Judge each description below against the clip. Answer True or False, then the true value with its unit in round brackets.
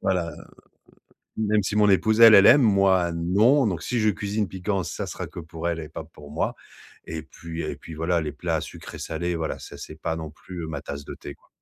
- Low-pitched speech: True (85 Hz)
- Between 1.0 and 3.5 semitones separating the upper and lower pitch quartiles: False (3.9 semitones)